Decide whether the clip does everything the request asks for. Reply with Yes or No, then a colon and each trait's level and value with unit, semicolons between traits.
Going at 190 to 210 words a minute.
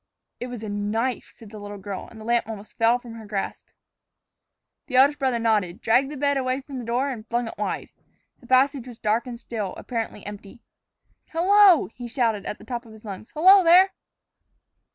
Yes: average, 200 wpm